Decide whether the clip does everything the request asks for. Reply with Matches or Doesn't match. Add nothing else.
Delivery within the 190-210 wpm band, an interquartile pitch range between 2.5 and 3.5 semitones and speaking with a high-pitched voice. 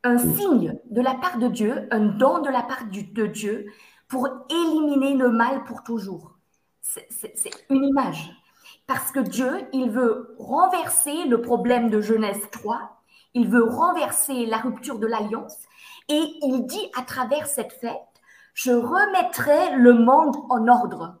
Doesn't match